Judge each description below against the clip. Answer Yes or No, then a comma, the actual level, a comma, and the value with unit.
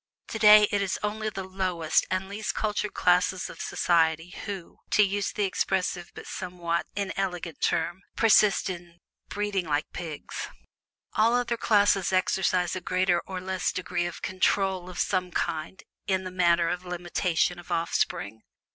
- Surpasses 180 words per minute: No, average, 150 wpm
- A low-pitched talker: No, medium, 185 Hz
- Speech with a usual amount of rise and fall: No, narrow, 2.3 semitones